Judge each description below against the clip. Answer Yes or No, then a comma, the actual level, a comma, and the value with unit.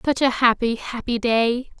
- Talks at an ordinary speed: Yes, average, 165 wpm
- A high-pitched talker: Yes, high, 240 Hz